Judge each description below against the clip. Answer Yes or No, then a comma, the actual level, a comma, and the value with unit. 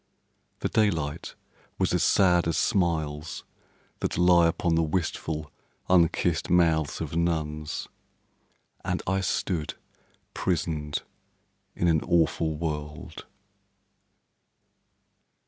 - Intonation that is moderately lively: No, narrow, 2.3 semitones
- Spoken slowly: Yes, slow, 95 wpm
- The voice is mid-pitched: No, very low, 85 Hz